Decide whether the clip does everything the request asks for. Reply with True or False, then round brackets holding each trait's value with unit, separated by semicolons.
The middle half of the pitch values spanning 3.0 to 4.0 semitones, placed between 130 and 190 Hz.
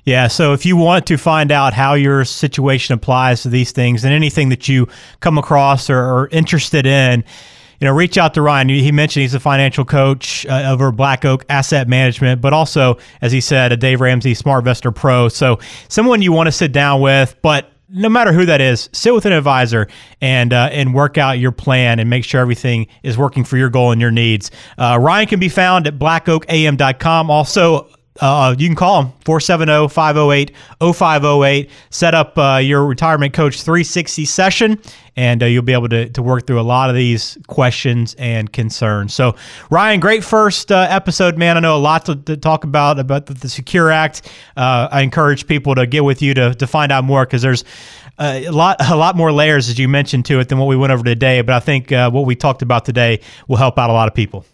True (3.6 semitones; 135 Hz)